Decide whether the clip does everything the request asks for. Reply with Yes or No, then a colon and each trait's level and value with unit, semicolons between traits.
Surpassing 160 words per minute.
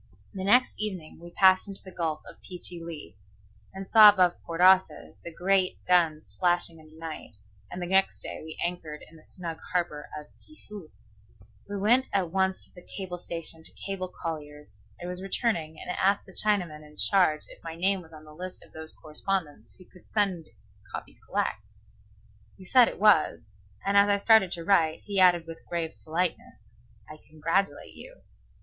Yes: average, 185 wpm